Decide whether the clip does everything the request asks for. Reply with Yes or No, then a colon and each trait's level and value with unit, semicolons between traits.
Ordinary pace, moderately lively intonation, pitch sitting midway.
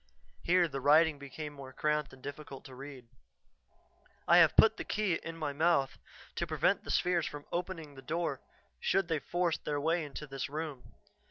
Yes: average, 180 wpm; average, 3.3 semitones; medium, 150 Hz